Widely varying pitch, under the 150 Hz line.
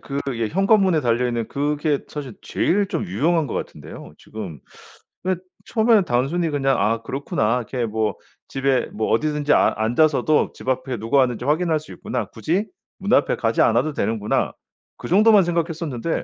Yes: wide, 6.2 semitones; medium, 140 Hz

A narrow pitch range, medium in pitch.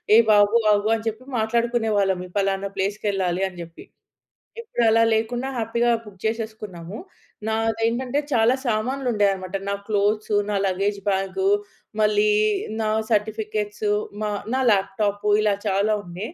No: narrow, 2.2 semitones; high, 210 Hz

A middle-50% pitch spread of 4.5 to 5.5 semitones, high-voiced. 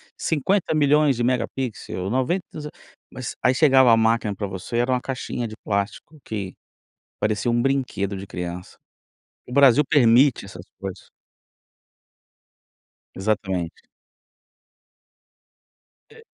No: average, 5.2 semitones; low, 120 Hz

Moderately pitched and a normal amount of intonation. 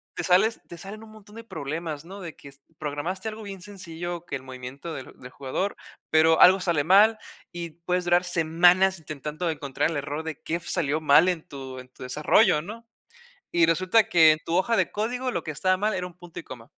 Yes: medium, 170 Hz; average, 3.7 semitones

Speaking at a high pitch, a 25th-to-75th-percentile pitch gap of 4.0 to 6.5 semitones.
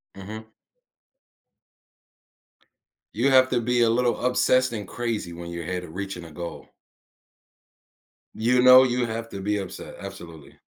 No: low, 110 Hz; wide, 5.4 semitones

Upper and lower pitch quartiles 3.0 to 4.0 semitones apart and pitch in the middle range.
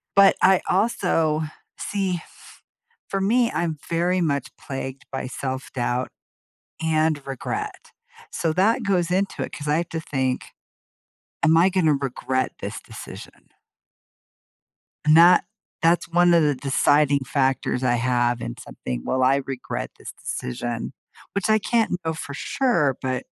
No: average, 5.3 semitones; medium, 155 Hz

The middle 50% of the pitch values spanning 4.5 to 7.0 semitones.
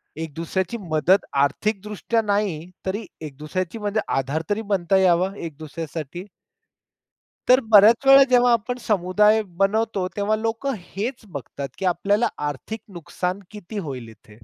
Yes: average, 5.0 semitones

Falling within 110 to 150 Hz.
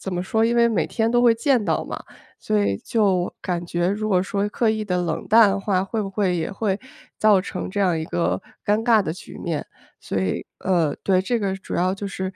No: high, 195 Hz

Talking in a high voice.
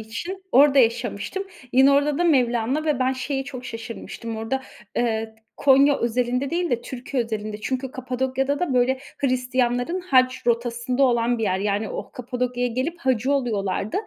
Yes: very high, 250 Hz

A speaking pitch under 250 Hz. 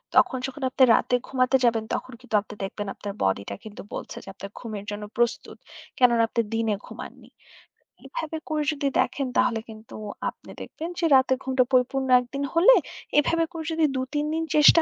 No: very high, 255 Hz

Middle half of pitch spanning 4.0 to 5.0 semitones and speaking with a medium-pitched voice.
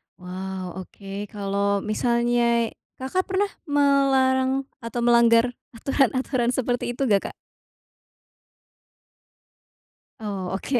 No: average, 4.5 semitones; high, 235 Hz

